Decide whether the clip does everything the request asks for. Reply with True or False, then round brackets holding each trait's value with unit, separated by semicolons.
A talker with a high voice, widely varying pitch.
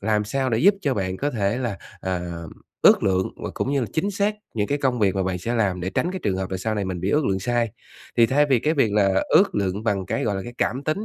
False (110 Hz; 5.9 semitones)